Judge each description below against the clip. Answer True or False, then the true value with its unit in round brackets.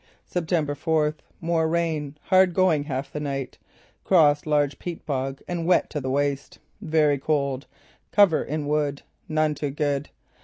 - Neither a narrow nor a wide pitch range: False (2.2 semitones)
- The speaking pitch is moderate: True (150 Hz)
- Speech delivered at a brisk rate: False (150 wpm)